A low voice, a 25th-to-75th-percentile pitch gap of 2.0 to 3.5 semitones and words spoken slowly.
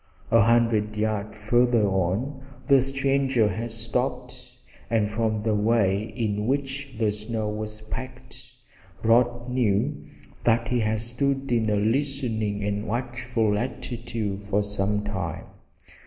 Yes: low, 115 Hz; average, 2.7 semitones; slow, 125 wpm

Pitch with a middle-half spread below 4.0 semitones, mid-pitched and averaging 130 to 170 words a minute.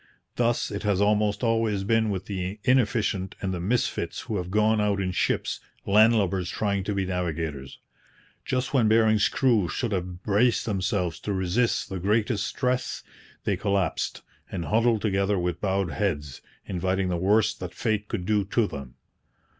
No: average, 3.0 semitones; low, 100 Hz; average, 165 wpm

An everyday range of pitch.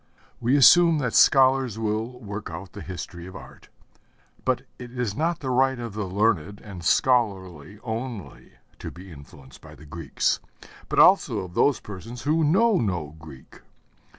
No: wide, 5.9 semitones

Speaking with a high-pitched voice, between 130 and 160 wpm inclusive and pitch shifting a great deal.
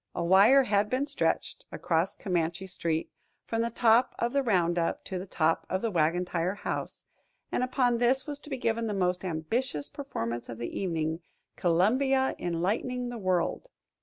No: high, 195 Hz; average, 170 wpm; wide, 6.3 semitones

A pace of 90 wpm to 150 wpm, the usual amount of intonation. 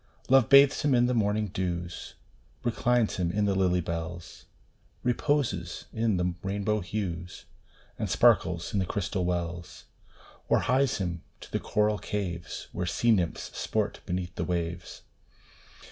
Yes: average, 145 wpm; average, 3.9 semitones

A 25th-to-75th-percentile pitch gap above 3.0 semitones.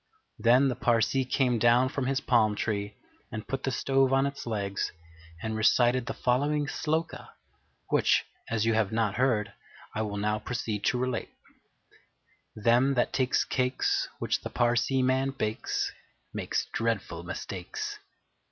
Yes: average, 3.4 semitones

